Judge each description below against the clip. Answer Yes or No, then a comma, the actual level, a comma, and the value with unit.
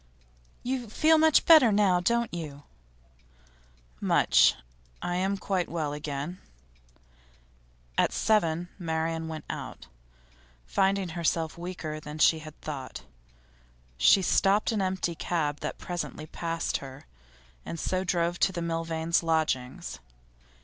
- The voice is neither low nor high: Yes, medium, 170 Hz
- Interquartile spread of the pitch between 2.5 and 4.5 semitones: Yes, average, 3.3 semitones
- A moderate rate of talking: No, slow, 120 wpm